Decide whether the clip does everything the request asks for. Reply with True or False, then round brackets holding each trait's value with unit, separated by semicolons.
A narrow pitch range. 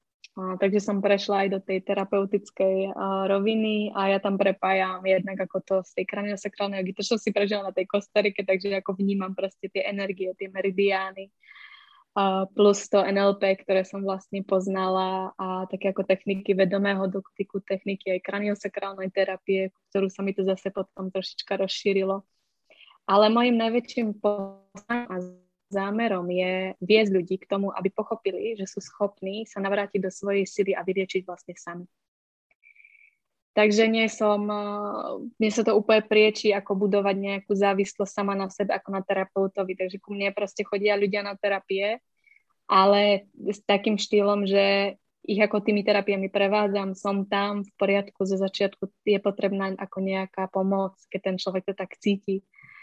True (1.2 semitones)